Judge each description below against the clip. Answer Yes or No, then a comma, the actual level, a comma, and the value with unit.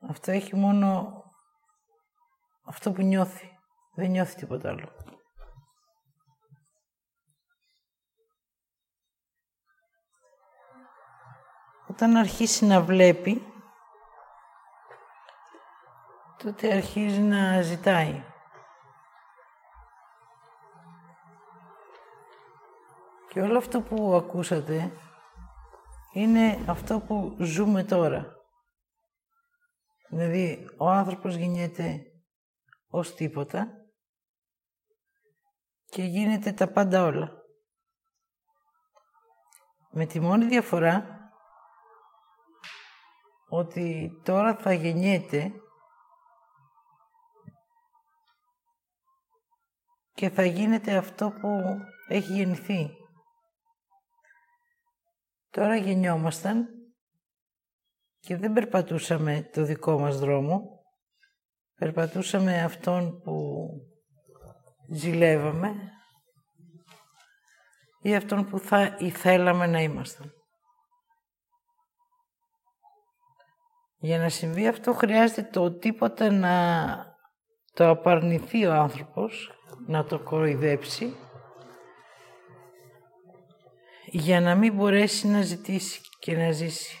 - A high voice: Yes, high, 195 Hz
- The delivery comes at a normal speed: No, slow, 70 wpm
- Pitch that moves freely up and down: Yes, wide, 6.5 semitones